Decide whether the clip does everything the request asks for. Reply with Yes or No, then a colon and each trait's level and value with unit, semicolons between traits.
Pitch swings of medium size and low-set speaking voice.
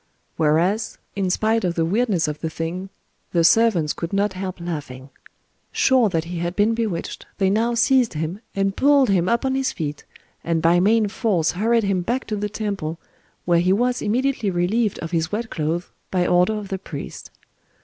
No: average, 4.8 semitones; high, 190 Hz